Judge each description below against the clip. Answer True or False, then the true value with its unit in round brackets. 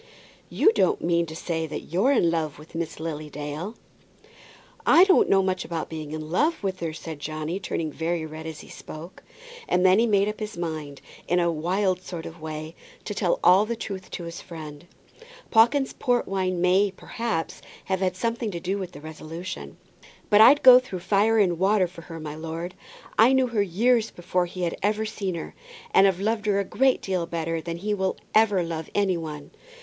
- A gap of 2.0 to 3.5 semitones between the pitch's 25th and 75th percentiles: False (4.1 semitones)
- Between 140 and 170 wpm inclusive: False (205 wpm)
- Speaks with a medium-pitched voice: True (180 Hz)